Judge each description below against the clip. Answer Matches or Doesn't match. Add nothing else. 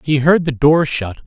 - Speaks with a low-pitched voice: Doesn't match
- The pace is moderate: Doesn't match